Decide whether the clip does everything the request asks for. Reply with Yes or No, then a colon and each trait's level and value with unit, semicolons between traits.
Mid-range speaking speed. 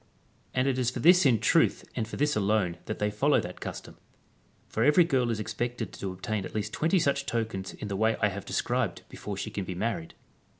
No: fast, 220 wpm